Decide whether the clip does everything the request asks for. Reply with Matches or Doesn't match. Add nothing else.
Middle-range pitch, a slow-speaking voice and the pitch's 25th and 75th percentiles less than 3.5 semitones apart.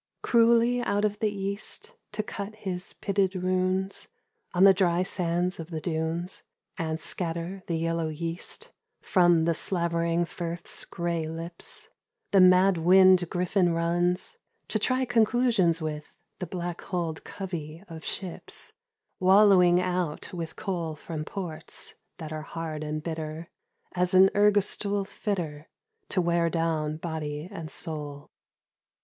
Matches